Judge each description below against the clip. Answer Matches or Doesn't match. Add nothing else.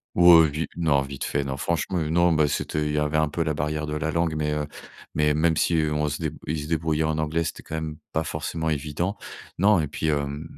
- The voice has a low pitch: Matches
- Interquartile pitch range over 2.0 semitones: Doesn't match